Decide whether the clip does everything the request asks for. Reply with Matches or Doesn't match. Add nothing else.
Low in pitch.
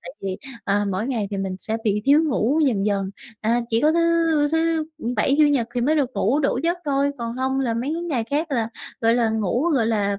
Doesn't match